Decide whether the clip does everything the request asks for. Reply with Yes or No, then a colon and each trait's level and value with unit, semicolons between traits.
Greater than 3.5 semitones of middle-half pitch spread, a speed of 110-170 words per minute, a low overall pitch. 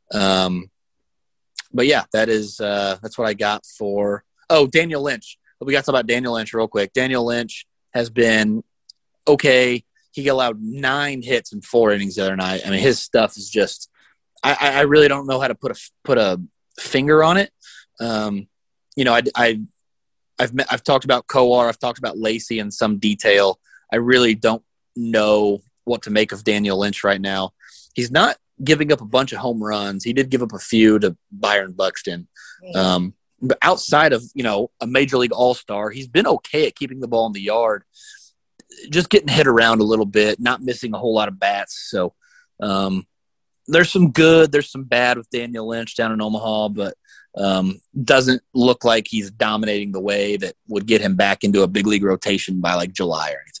No: average, 4.4 semitones; average, 200 wpm; low, 115 Hz